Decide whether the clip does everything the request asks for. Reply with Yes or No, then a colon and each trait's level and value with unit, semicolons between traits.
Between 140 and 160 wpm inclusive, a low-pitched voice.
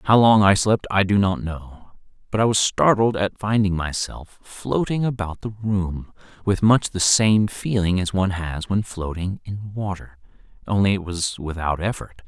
No: average, 175 wpm; low, 100 Hz